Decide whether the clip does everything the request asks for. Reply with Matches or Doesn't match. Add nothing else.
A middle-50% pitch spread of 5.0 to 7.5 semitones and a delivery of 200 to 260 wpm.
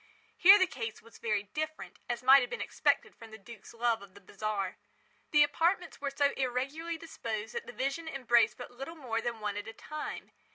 Matches